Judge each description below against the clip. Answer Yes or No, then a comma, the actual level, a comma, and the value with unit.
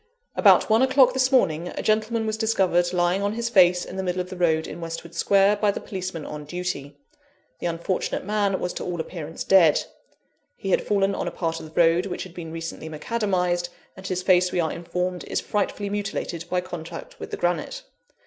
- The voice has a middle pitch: Yes, medium, 180 Hz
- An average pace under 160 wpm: No, fast, 205 wpm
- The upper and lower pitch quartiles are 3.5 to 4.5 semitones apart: No, average, 3.0 semitones